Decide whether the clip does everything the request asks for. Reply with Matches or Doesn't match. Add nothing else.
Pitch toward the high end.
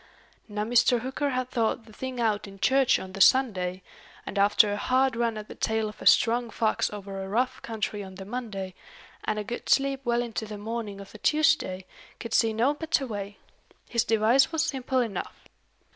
Matches